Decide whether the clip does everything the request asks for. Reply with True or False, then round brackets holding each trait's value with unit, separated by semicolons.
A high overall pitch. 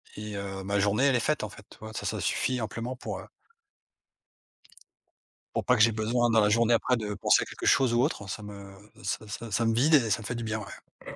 False (110 Hz)